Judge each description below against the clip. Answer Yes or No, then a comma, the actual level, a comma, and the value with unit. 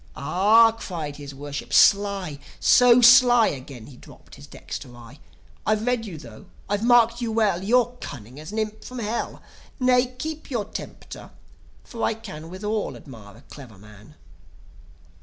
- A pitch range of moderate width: No, wide, 8.6 semitones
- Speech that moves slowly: No, average, 160 wpm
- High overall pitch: Yes, high, 205 Hz